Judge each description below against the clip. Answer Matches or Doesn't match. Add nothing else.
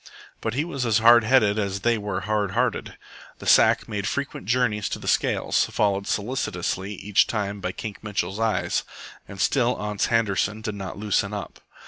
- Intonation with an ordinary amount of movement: Doesn't match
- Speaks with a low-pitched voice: Matches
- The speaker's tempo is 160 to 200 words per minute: Matches